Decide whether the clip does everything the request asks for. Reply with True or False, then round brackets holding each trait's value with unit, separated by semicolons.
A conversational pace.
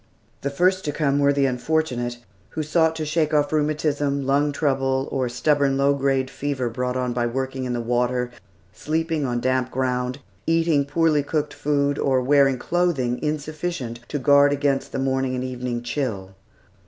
True (170 wpm)